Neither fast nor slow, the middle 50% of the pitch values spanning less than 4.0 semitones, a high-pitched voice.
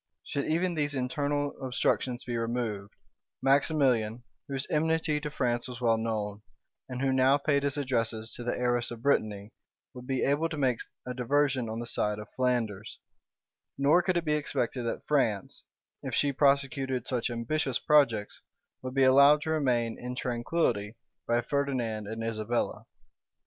No: average, 160 wpm; average, 3.5 semitones; low, 125 Hz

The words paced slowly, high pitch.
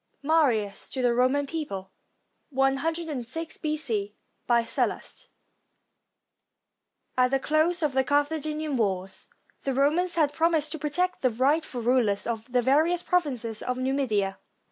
Yes: slow, 130 wpm; very high, 270 Hz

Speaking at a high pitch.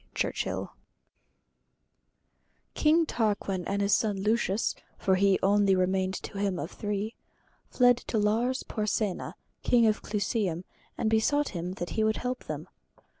Yes: high, 210 Hz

